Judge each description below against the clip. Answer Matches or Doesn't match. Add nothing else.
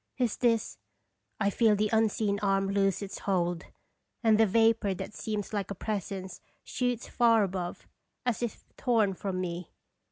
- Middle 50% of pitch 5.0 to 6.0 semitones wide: Doesn't match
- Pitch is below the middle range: Doesn't match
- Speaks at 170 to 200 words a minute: Doesn't match